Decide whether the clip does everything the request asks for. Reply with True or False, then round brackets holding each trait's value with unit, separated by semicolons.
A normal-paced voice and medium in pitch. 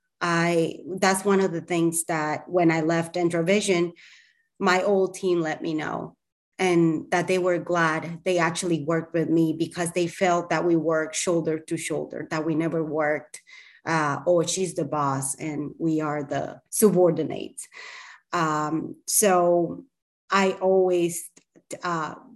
True (150 wpm; 170 Hz)